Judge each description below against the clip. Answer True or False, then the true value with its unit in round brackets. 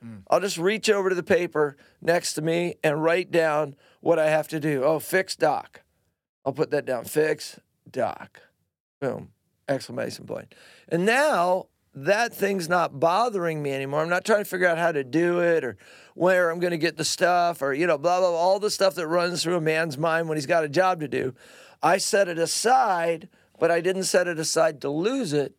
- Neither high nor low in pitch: True (170 Hz)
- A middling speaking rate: False (215 wpm)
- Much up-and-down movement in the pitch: False (2.9 semitones)